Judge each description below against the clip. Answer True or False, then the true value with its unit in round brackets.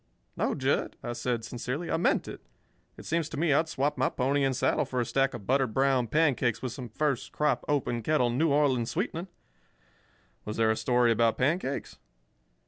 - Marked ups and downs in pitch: False (3.6 semitones)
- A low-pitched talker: True (130 Hz)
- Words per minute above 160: True (190 wpm)